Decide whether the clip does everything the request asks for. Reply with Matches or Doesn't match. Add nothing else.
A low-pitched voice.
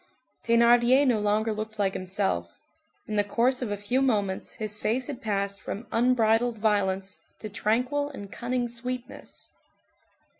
Doesn't match